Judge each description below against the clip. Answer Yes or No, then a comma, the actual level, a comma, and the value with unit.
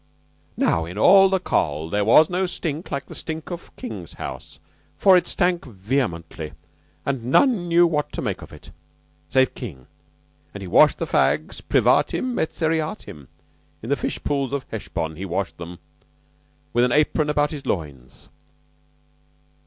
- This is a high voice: No, low, 135 Hz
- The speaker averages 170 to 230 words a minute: No, average, 155 wpm